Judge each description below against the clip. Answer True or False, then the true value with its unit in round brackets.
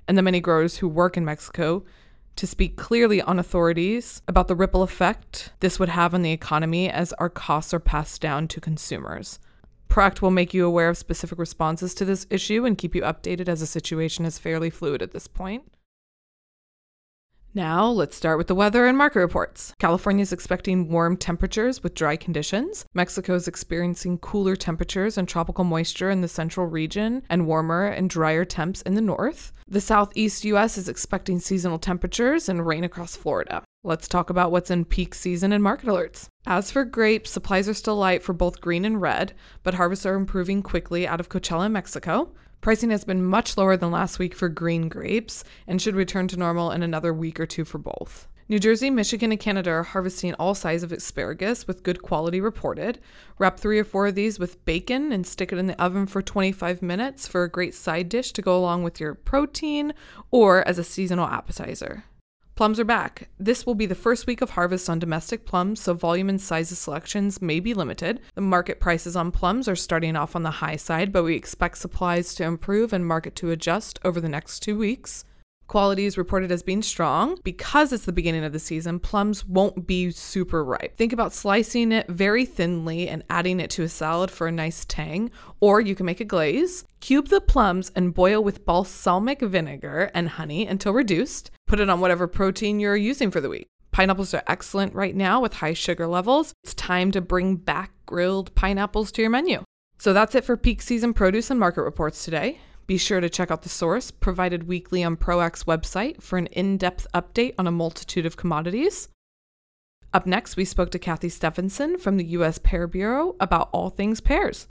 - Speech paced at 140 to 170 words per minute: False (200 wpm)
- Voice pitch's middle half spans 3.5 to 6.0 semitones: False (3.1 semitones)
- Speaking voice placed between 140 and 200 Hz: True (185 Hz)